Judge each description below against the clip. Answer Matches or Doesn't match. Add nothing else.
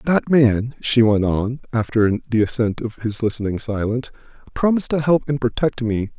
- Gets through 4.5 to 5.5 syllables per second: Matches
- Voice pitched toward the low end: Matches